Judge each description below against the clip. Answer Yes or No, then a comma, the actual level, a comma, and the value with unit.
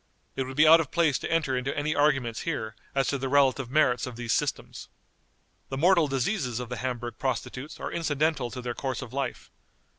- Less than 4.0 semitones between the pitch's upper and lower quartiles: Yes, average, 3.4 semitones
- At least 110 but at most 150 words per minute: No, fast, 205 wpm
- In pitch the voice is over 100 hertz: Yes, low, 135 Hz